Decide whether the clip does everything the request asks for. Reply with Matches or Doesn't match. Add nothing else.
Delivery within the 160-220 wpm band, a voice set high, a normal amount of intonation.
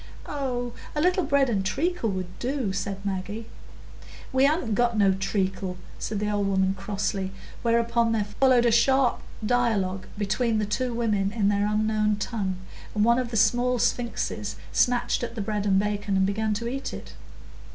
Matches